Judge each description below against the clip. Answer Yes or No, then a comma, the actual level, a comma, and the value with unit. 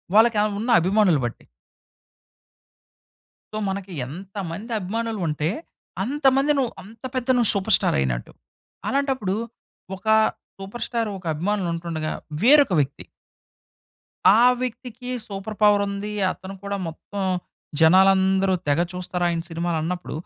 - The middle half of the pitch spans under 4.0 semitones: No, average, 4.4 semitones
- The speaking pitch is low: No, high, 195 Hz